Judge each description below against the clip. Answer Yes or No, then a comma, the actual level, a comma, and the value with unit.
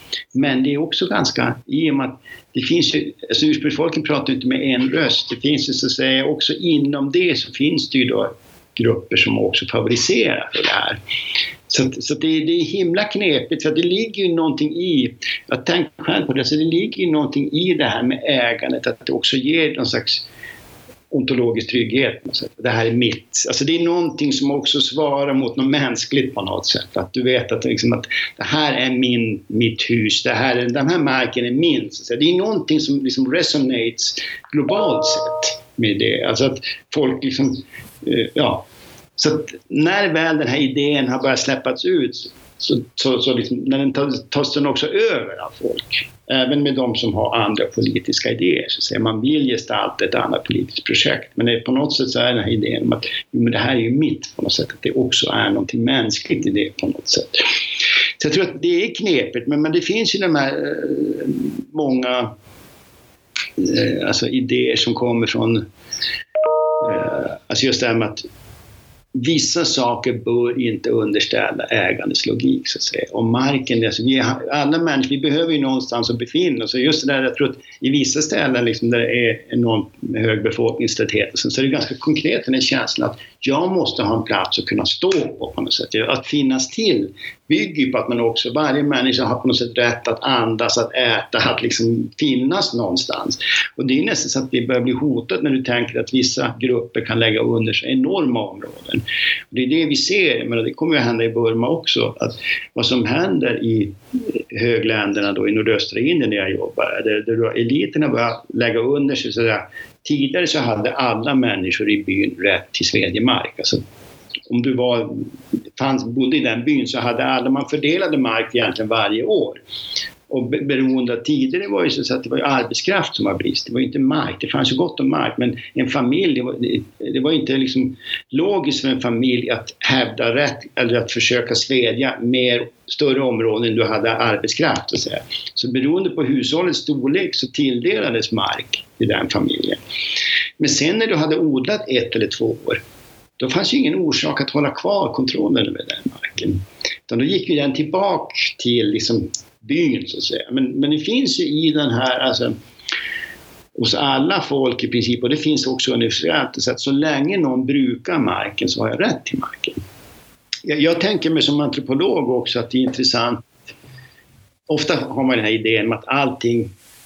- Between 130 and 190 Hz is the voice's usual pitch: Yes, low, 135 Hz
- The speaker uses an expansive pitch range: Yes, wide, 6.4 semitones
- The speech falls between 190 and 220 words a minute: Yes, fast, 195 wpm